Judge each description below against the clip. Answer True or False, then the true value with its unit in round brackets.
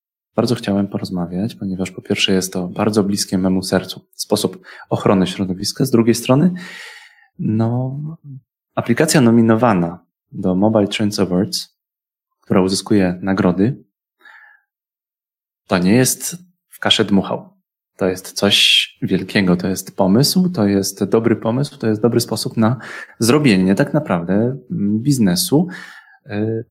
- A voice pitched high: False (110 Hz)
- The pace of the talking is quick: False (120 wpm)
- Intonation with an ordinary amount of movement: False (5.7 semitones)